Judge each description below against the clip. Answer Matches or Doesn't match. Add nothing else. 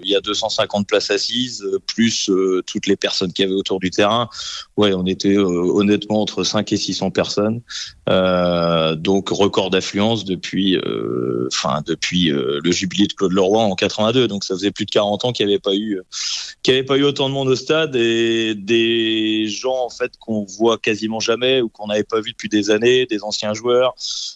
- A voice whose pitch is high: Doesn't match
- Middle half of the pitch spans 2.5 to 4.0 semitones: Matches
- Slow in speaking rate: Doesn't match